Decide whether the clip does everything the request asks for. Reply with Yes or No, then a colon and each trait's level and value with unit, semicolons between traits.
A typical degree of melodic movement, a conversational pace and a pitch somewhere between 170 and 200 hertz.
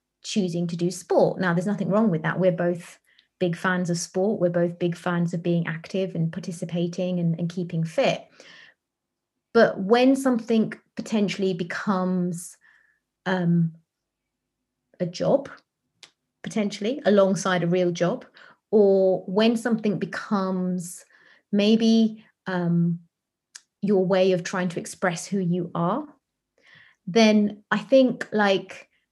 No: average, 3.3 semitones; slow, 125 wpm; medium, 185 Hz